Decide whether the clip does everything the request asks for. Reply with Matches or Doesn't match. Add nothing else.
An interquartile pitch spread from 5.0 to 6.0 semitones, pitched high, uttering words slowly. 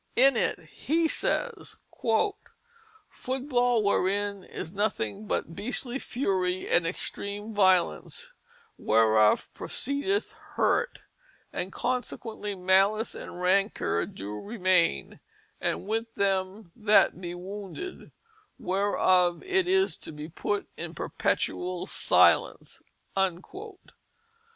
Matches